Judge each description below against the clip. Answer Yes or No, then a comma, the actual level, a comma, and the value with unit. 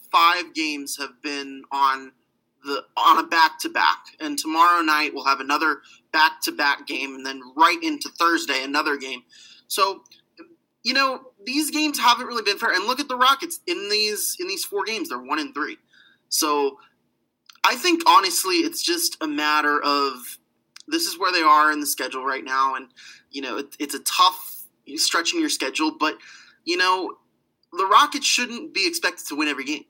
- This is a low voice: No, high, 235 Hz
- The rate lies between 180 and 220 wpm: Yes, average, 190 wpm